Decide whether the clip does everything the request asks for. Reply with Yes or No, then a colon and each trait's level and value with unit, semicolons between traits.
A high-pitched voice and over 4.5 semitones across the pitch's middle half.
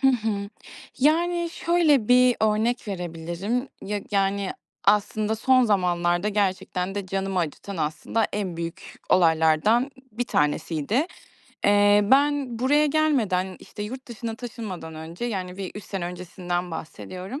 Yes: high, 205 Hz; average, 5.3 semitones